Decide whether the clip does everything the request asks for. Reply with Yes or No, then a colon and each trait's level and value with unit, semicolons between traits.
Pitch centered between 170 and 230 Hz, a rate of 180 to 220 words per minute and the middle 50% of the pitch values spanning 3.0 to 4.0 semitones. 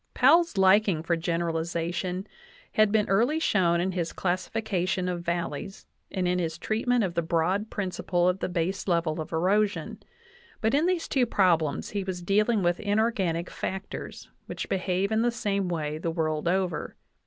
No: medium, 185 Hz; average, 165 wpm; average, 3.5 semitones